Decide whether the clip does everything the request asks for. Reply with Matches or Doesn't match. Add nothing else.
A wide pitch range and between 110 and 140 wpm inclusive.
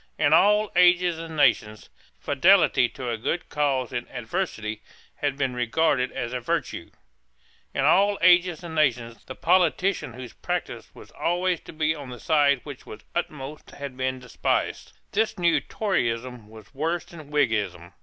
Doesn't match